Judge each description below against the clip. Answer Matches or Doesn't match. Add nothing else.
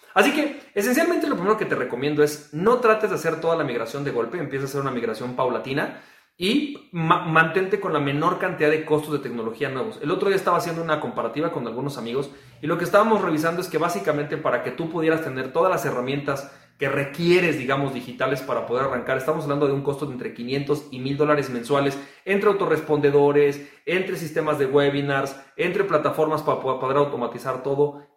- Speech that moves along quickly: Matches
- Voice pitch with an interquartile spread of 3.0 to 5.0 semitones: Matches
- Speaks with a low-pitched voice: Doesn't match